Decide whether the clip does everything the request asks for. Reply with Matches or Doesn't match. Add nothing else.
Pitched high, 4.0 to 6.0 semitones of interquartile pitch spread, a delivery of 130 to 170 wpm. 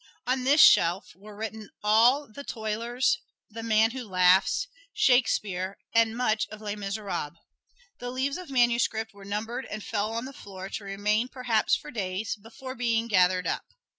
Doesn't match